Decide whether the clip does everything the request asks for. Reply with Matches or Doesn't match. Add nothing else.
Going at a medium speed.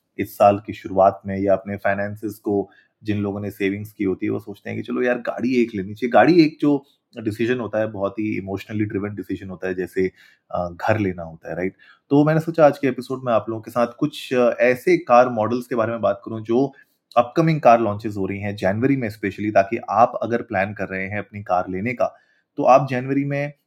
Doesn't match